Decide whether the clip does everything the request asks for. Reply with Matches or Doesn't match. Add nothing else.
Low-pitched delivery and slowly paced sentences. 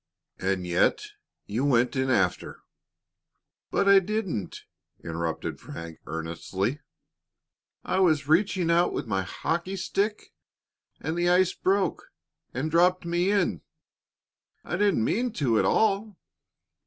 Doesn't match